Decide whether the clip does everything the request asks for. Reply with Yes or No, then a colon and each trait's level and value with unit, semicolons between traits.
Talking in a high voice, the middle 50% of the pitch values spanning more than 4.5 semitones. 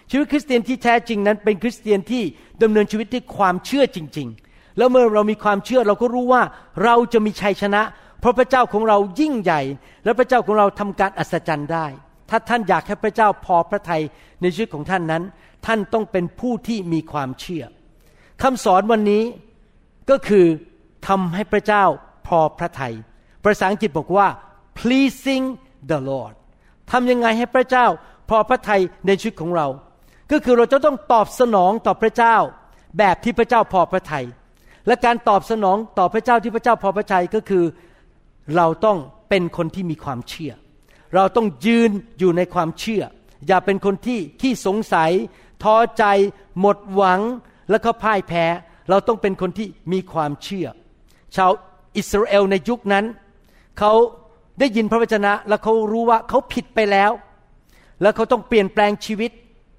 No: high, 205 Hz; average, 4.2 semitones